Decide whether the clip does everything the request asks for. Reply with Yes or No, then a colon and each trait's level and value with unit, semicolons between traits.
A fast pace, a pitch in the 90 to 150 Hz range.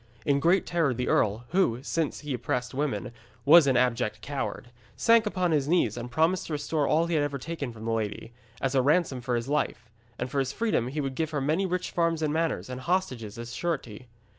Yes: fast, 220 wpm; medium, 140 Hz